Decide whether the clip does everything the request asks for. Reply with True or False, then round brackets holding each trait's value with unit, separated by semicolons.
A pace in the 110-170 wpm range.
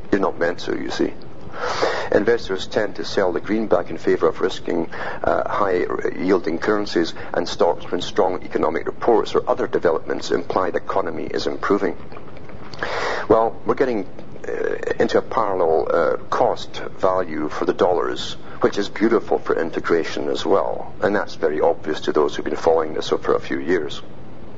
True (165 wpm)